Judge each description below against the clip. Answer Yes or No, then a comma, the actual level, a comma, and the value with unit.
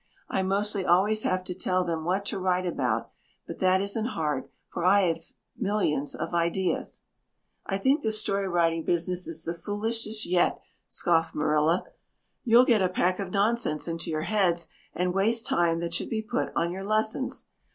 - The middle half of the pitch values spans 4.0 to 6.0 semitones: No, average, 3.6 semitones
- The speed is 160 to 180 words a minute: Yes, average, 170 wpm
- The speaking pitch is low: No, medium, 185 Hz